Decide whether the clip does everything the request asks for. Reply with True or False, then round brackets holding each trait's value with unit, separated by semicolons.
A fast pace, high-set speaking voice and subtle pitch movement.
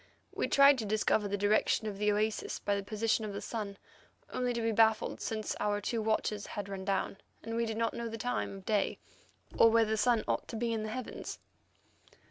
True (220 wpm; 215 Hz; 1.8 semitones)